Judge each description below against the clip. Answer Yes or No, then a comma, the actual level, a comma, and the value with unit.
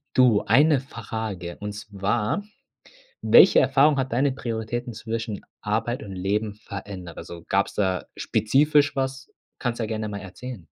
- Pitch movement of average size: Yes, average, 4.1 semitones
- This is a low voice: Yes, low, 110 Hz